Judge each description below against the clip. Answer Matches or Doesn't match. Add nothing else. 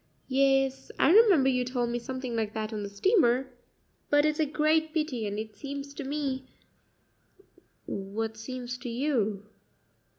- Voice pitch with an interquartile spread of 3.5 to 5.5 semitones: Matches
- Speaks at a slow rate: Doesn't match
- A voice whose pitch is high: Matches